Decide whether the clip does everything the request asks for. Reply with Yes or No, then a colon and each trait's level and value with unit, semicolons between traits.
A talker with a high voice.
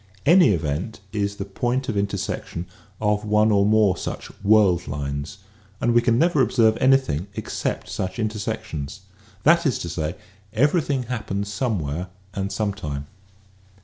No: low, 105 Hz